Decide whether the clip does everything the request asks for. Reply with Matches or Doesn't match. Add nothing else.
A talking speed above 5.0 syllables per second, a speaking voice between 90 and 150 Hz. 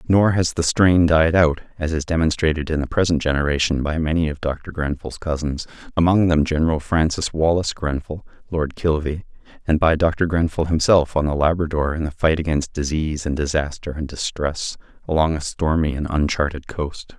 Doesn't match